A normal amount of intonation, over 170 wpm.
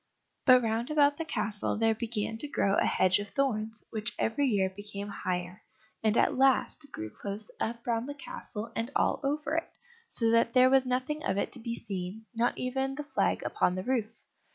Yes: average, 4.2 semitones; average, 200 wpm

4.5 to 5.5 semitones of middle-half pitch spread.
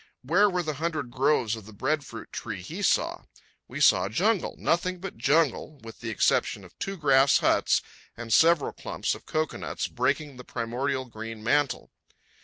Yes: average, 5.2 semitones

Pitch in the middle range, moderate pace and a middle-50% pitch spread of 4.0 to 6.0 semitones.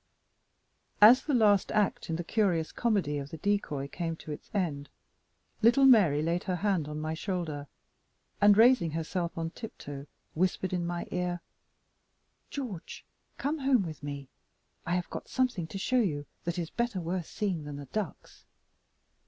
Yes: medium, 175 Hz; average, 160 wpm; average, 5.0 semitones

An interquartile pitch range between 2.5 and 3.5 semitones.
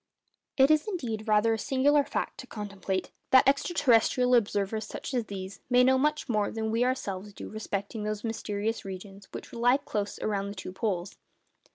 No: average, 3.9 semitones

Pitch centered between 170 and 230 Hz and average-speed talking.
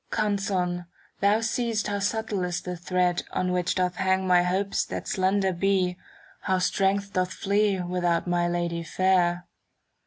Yes: medium, 185 Hz; average, 155 wpm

